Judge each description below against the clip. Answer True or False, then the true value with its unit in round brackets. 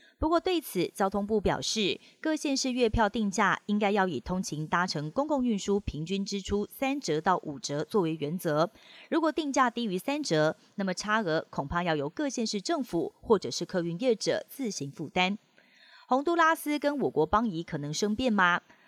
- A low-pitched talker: False (200 Hz)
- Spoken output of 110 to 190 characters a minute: False (275 characters per minute)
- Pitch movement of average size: False (7.3 semitones)